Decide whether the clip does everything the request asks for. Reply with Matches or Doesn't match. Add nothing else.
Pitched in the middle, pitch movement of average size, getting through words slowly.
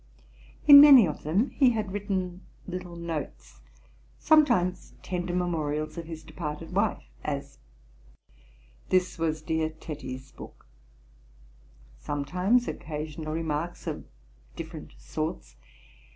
Matches